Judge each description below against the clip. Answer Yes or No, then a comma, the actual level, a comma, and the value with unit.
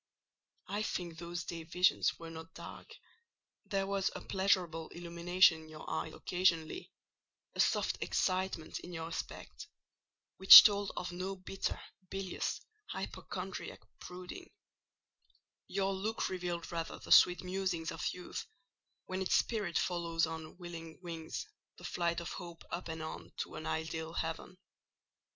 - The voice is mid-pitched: Yes, medium, 175 Hz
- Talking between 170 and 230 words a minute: No, slow, 135 wpm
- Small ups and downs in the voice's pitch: Yes, narrow, 2.3 semitones